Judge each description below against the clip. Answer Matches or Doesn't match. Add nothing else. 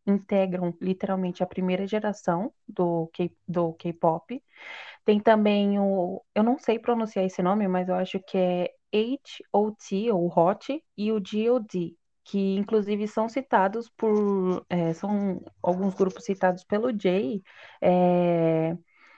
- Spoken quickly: Doesn't match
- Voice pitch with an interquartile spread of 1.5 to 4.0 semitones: Matches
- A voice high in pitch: Matches